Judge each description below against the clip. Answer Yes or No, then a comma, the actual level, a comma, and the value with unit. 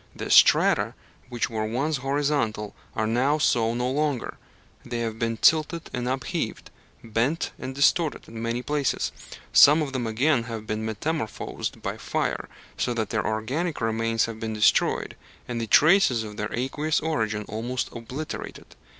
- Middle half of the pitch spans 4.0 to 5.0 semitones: Yes, average, 4.4 semitones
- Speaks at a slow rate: No, average, 155 wpm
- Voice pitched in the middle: No, low, 120 Hz